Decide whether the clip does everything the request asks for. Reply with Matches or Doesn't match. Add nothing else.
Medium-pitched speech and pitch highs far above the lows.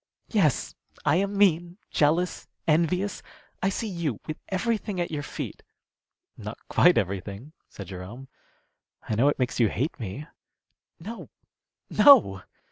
Matches